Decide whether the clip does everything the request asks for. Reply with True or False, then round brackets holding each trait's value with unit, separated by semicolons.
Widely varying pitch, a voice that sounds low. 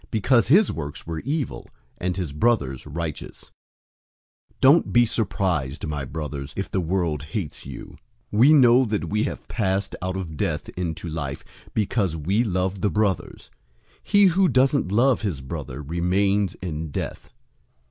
True (6.3 semitones; 95 Hz)